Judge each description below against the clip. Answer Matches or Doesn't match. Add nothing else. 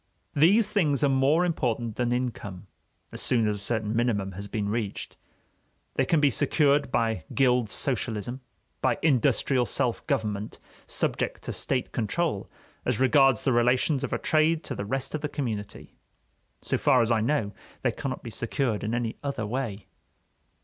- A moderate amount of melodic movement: Matches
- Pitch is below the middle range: Matches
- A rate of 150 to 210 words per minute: Matches